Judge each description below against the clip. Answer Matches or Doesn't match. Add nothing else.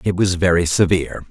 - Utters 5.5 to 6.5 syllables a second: Matches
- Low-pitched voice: Matches